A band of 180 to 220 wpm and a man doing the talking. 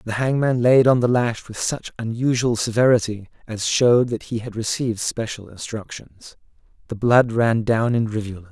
No: average, 170 wpm; male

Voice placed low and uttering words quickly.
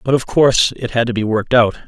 Yes: low, 120 Hz; fast, 290 wpm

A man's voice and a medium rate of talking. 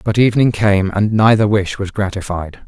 Yes: male; average, 180 wpm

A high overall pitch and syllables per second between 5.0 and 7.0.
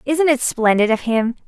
No: very high, 250 Hz; 4.7 syllables/s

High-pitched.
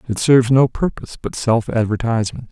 No: low, 120 Hz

